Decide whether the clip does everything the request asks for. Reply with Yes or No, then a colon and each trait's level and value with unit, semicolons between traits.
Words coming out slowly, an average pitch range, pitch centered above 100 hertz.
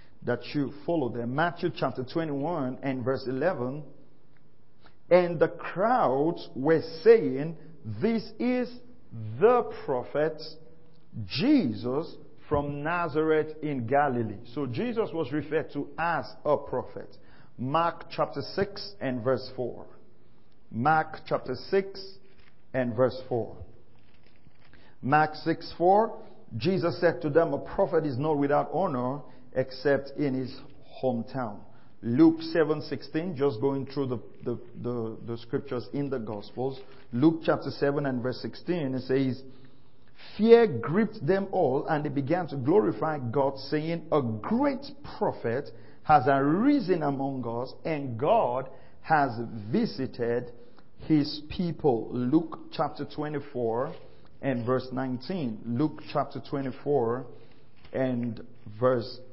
Yes: slow, 120 wpm; average, 4.2 semitones; medium, 140 Hz